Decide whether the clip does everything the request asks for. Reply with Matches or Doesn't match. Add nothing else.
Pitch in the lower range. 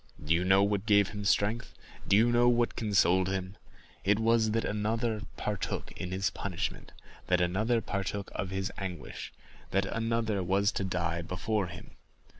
Matches